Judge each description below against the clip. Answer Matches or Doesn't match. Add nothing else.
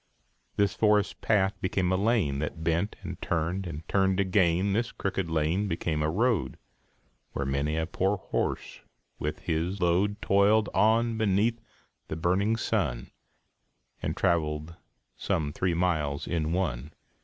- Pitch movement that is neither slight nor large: Matches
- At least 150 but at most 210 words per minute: Doesn't match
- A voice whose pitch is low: Matches